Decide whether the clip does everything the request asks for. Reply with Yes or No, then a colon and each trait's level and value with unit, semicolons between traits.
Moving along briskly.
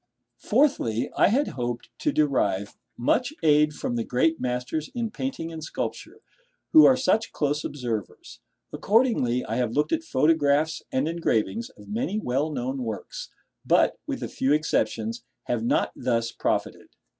No: average, 150 wpm